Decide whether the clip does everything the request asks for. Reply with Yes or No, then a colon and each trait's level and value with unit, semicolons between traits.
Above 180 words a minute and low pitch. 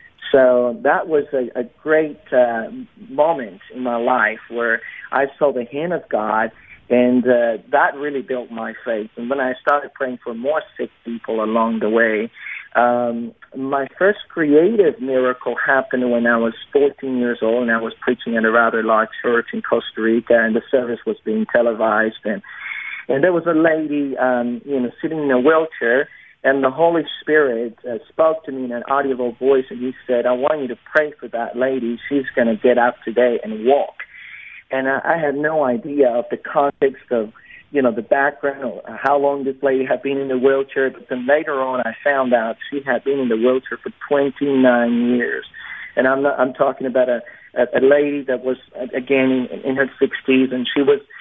Yes: average, 200 wpm; low, 130 Hz